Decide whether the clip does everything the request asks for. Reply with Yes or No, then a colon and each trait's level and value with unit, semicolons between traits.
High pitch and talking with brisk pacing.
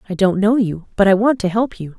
Yes: high, 200 Hz; fast, 300 wpm